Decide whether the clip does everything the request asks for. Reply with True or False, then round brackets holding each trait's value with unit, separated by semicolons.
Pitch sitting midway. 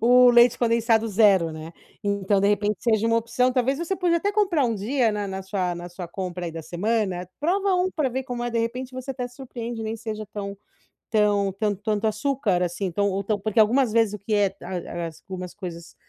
False (215 Hz)